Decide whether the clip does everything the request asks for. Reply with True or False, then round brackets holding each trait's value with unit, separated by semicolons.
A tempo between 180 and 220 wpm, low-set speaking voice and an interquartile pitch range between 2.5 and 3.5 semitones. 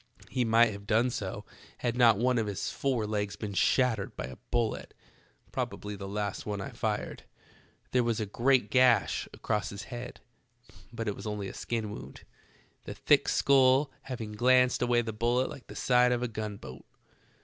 True (185 wpm; 115 Hz; 3.0 semitones)